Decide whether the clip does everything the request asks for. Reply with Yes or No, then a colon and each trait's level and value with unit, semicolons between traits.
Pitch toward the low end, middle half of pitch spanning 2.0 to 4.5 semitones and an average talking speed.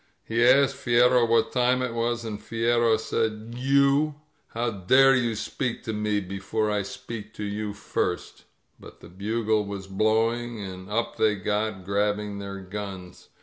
Yes: low, 110 Hz; narrow, 2.6 semitones; average, 165 wpm